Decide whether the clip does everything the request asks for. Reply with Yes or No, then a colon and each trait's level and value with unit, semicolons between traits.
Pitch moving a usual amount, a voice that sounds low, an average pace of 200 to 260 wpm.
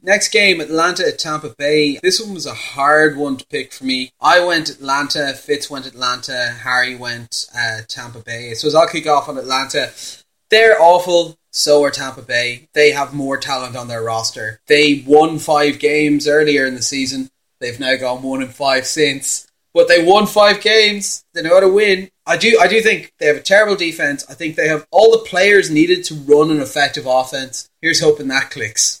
No: average, 4.6 semitones; medium, 150 Hz; fast, 205 wpm